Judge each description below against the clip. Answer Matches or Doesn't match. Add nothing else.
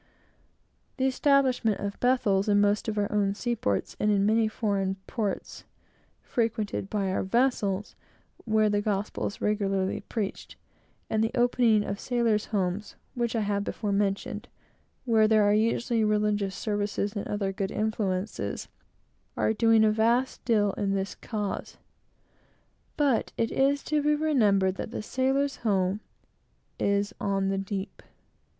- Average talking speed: Matches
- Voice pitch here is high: Matches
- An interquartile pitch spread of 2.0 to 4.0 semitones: Matches